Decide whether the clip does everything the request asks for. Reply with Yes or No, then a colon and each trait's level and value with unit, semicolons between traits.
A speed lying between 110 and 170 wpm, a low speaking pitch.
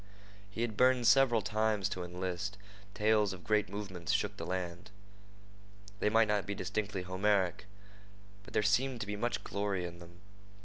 Yes: average, 165 wpm; low, 105 Hz